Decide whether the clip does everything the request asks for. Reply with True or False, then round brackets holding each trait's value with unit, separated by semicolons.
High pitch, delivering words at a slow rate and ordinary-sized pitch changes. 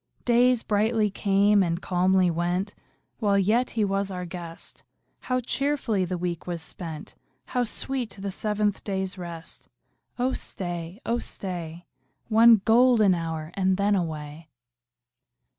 True (195 Hz; 130 wpm; 3.9 semitones)